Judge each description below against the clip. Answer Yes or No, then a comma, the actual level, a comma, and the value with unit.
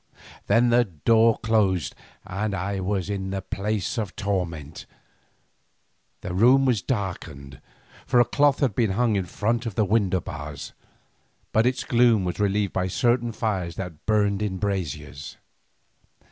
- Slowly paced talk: No, average, 145 wpm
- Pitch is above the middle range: No, low, 100 Hz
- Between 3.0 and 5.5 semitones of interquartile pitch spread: Yes, average, 3.7 semitones